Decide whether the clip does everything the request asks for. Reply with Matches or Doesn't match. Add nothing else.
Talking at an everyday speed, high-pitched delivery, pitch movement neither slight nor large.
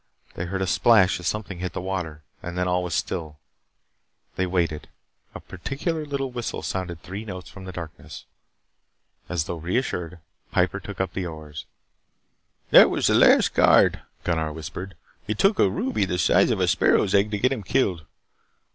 Doesn't match